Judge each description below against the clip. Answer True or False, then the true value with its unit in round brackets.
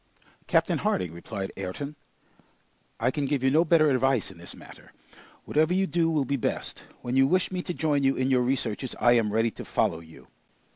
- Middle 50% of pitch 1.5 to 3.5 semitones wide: False (5.2 semitones)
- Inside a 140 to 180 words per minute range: False (200 wpm)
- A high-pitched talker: False (135 Hz)